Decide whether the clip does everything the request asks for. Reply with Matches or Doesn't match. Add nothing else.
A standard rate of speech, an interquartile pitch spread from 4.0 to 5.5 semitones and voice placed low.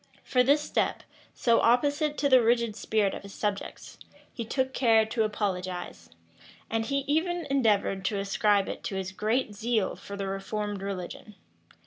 Doesn't match